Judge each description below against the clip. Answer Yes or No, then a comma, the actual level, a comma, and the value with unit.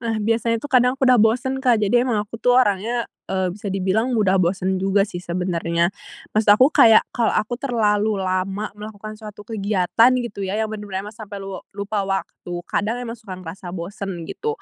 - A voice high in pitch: Yes, high, 210 Hz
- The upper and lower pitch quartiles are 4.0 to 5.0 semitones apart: No, average, 3.1 semitones